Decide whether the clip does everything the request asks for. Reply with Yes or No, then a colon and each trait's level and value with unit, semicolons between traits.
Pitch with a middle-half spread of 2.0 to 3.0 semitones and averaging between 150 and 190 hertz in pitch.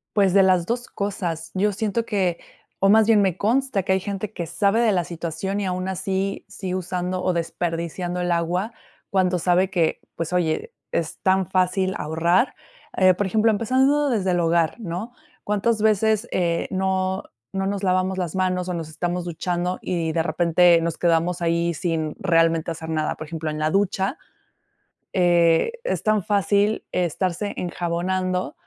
Yes: average, 2.7 semitones; medium, 185 Hz